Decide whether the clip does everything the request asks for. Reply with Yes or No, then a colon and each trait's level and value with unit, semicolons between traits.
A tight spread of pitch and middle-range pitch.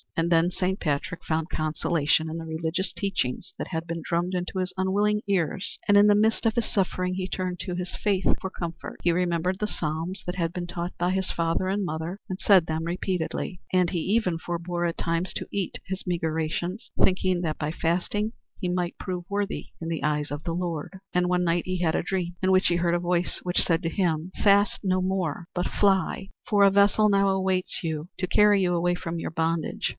Yes: narrow, 2.2 semitones; medium, 180 Hz